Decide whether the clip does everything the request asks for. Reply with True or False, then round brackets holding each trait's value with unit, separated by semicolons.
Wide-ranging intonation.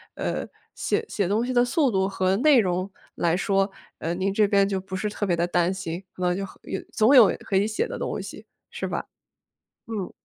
False (2.8 semitones)